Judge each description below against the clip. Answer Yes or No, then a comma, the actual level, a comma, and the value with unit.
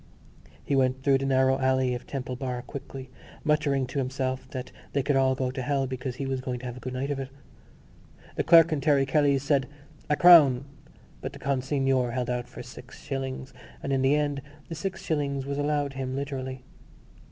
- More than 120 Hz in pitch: Yes, low, 135 Hz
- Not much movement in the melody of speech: Yes, narrow, 1.5 semitones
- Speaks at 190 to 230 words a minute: Yes, average, 200 wpm